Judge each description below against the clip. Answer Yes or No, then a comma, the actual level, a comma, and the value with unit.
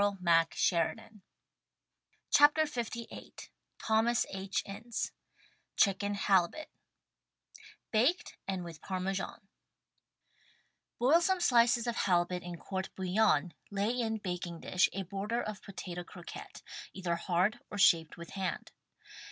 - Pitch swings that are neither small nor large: Yes, average, 4.3 semitones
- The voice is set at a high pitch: Yes, high, 195 Hz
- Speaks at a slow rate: Yes, slow, 120 wpm